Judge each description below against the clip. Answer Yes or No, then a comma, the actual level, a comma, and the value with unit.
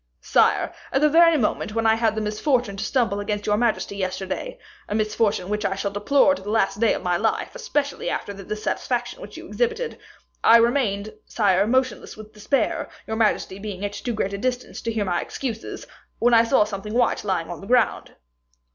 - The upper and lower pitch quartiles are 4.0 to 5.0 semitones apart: No, average, 3.5 semitones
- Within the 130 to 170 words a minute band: No, average, 200 wpm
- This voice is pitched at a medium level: No, high, 215 Hz